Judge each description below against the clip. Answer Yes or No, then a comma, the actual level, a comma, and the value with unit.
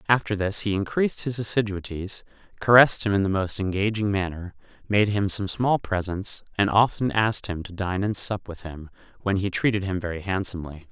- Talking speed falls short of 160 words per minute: No, average, 185 wpm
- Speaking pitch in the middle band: No, low, 100 Hz